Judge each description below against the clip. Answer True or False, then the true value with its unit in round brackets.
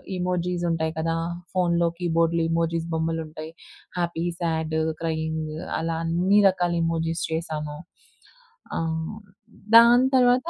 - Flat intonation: True (1.6 semitones)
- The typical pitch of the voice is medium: True (165 Hz)